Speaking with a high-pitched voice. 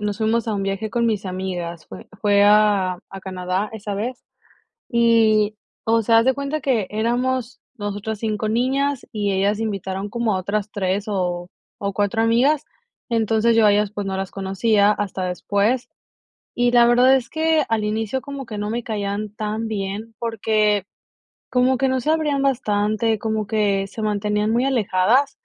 Yes: high, 215 Hz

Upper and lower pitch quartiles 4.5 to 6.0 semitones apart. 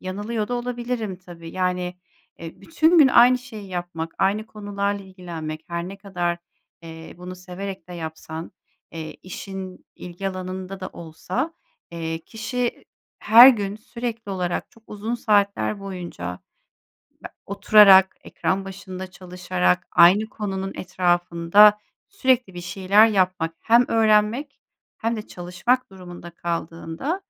No: average, 3.6 semitones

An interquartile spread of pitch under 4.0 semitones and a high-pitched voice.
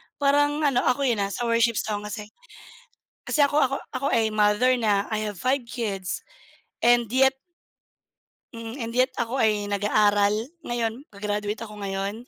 Yes: average, 3.4 semitones; high, 225 Hz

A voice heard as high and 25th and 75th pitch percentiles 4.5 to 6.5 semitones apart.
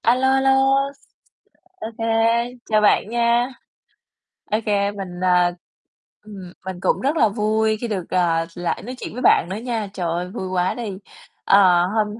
No: high, 210 Hz; average, 4.1 semitones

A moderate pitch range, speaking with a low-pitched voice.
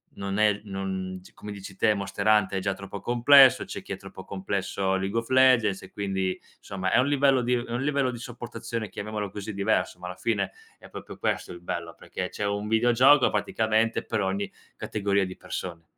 Yes: average, 3.4 semitones; low, 100 Hz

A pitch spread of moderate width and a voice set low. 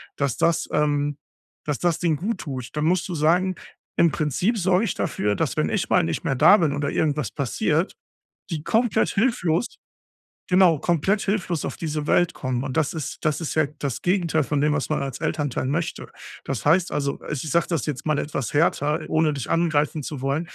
No: average, 3.2 semitones; medium, 155 Hz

